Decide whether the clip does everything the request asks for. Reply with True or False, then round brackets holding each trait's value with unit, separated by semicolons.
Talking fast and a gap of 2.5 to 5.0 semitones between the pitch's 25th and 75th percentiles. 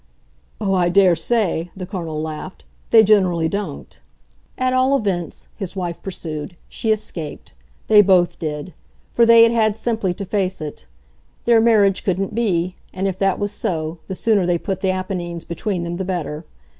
False (170 wpm; 3.4 semitones)